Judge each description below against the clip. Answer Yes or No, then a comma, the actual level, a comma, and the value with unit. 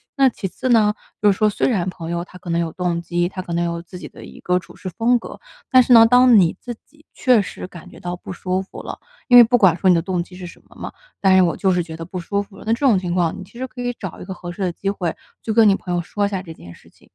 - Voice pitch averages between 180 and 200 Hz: Yes, medium, 185 Hz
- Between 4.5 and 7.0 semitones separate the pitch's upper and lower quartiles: No, average, 4.0 semitones